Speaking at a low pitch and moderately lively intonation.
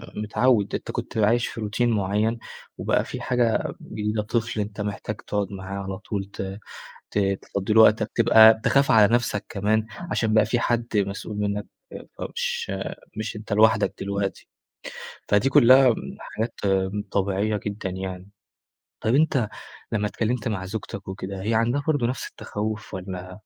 No: low, 105 Hz; narrow, 2.3 semitones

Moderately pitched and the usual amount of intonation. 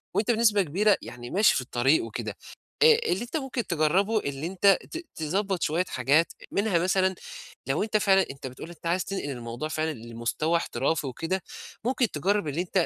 No: medium, 175 Hz; wide, 5.7 semitones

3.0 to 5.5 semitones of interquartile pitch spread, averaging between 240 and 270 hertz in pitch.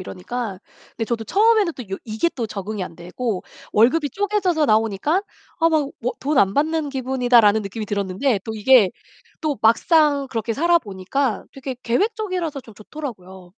No: wide, 6.5 semitones; very high, 250 Hz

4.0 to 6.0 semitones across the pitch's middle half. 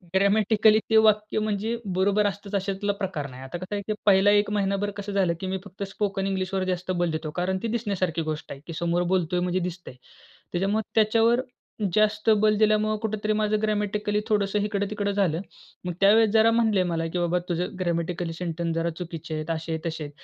No: average, 3.2 semitones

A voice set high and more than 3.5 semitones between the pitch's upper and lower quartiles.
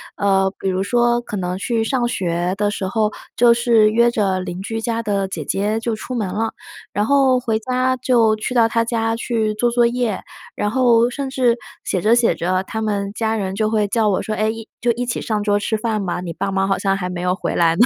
No: high, 220 Hz; average, 3.2 semitones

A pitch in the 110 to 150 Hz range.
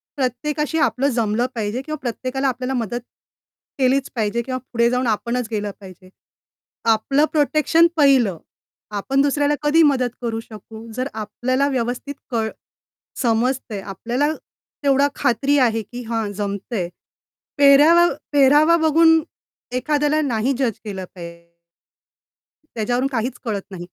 No: very high, 250 Hz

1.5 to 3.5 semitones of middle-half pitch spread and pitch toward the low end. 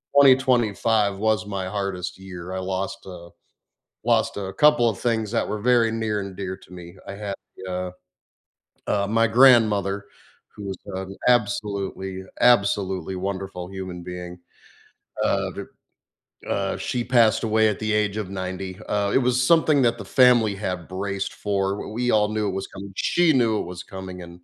Yes: average, 2.8 semitones; low, 100 Hz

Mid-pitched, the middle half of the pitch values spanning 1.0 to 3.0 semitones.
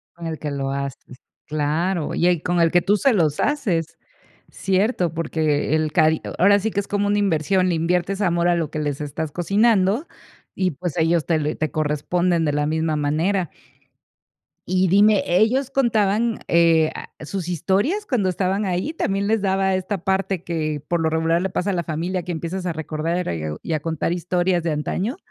No: medium, 175 Hz; average, 3.6 semitones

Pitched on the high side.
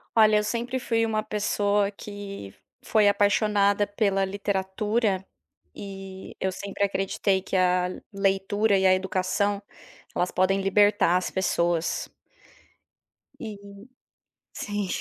Yes: high, 200 Hz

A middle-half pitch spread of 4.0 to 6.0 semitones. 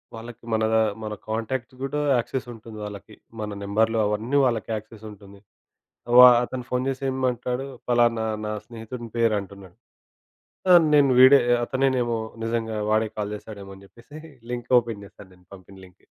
No: average, 2.9 semitones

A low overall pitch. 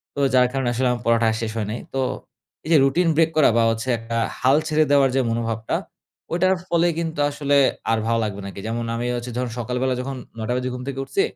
Yes: low, 125 Hz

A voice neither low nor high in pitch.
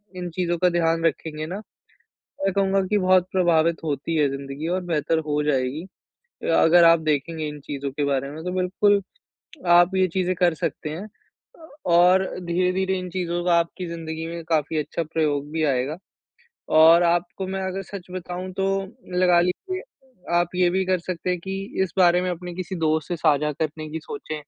Yes: medium, 170 Hz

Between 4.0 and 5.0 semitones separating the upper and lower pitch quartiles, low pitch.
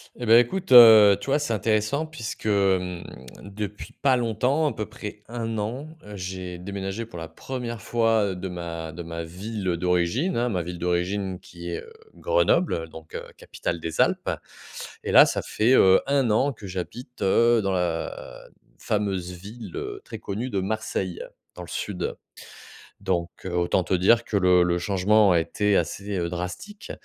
Yes: average, 4.6 semitones; low, 100 Hz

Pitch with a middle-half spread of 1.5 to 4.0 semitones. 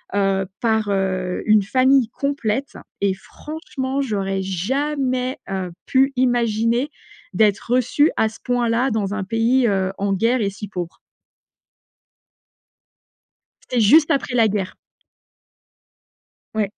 No: average, 4.7 semitones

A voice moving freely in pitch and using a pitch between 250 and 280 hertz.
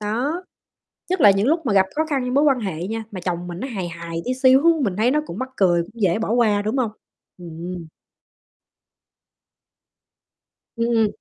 No: wide, 6.1 semitones; high, 215 Hz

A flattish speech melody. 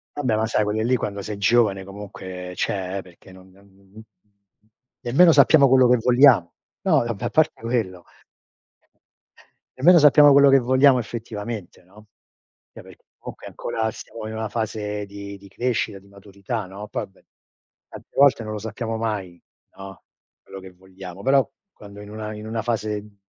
No: average, 3.6 semitones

